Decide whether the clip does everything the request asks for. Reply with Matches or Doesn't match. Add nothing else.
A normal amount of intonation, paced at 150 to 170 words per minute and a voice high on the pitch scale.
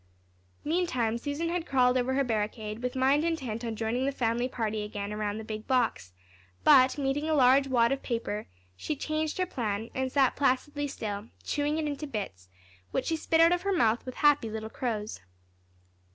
Doesn't match